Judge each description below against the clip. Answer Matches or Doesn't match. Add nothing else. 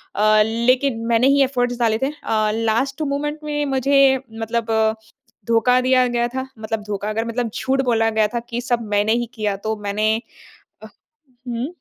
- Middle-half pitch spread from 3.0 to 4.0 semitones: Doesn't match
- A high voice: Matches